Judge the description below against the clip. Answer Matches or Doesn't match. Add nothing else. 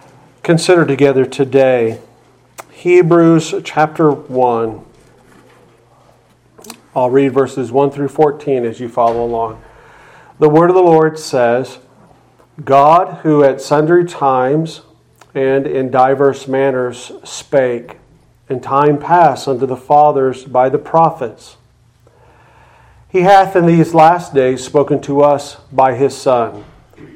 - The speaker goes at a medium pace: Doesn't match